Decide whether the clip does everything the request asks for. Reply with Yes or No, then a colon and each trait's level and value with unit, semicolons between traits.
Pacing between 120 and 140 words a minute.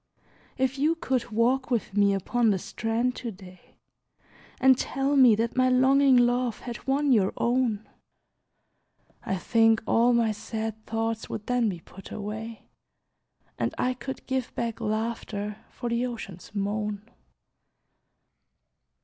Yes: slow, 135 wpm